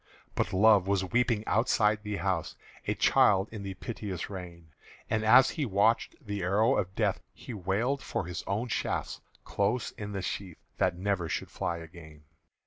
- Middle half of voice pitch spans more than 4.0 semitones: No, average, 3.1 semitones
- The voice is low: Yes, low, 100 Hz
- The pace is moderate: Yes, average, 170 wpm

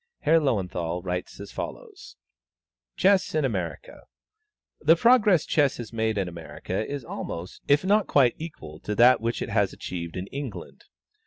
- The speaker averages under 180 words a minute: Yes, average, 155 wpm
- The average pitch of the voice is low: Yes, low, 115 Hz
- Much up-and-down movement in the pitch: Yes, wide, 8.9 semitones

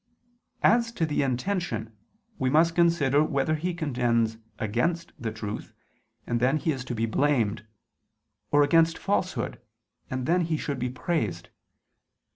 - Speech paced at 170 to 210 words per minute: No, average, 140 wpm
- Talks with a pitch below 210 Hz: Yes, medium, 140 Hz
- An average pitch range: No, wide, 5.8 semitones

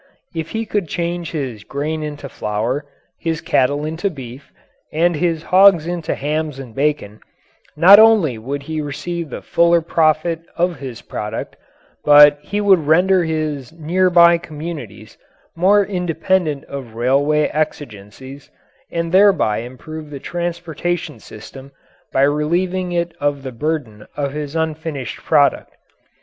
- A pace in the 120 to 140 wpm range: Yes, slow, 135 wpm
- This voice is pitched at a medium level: Yes, medium, 155 Hz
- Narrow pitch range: No, average, 3.7 semitones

